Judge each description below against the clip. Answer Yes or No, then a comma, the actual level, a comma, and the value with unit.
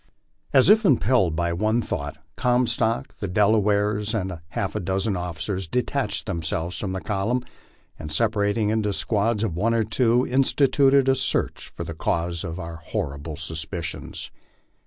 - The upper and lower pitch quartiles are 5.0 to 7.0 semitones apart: Yes, wide, 5.4 semitones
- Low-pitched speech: Yes, low, 105 Hz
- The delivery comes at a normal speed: Yes, average, 150 wpm